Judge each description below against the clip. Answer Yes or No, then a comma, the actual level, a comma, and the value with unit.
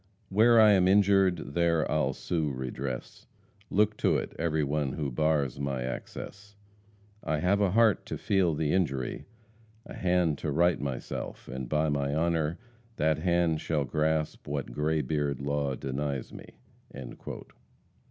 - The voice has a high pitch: No, very low, 80 Hz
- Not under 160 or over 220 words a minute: No, average, 145 wpm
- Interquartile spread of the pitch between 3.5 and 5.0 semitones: Yes, average, 4.0 semitones